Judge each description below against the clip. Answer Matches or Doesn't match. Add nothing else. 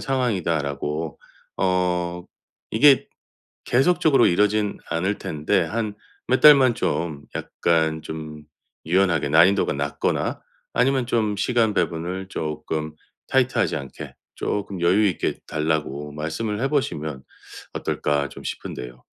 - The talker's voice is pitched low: Matches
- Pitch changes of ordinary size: Doesn't match